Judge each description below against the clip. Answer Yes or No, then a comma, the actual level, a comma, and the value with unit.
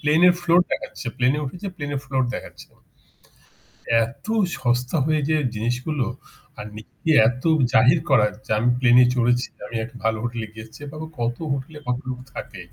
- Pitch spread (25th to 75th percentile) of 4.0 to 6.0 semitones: No, average, 3.3 semitones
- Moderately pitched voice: No, low, 125 Hz